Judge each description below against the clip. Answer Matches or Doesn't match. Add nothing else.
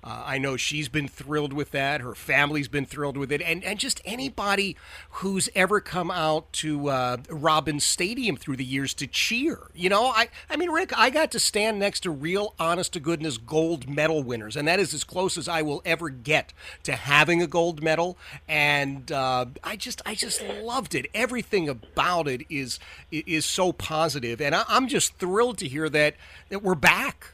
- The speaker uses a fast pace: Doesn't match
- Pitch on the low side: Doesn't match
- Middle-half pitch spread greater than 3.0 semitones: Matches